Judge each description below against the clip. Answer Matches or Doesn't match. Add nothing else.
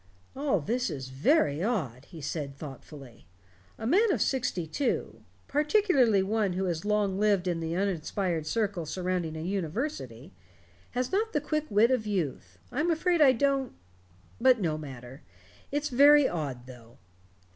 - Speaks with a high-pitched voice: Matches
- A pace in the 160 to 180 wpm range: Doesn't match